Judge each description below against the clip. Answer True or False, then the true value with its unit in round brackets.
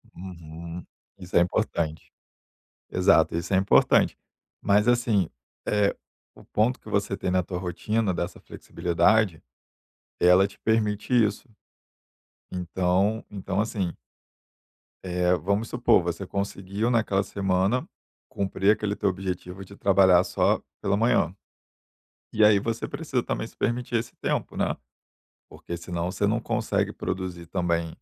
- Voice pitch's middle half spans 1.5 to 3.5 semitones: True (3.0 semitones)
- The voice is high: False (95 Hz)